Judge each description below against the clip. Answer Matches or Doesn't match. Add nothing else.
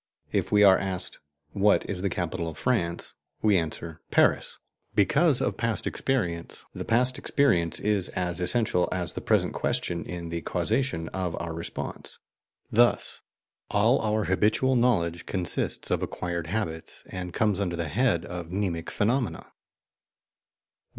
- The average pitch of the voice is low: Matches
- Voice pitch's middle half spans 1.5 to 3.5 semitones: Doesn't match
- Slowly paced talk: Doesn't match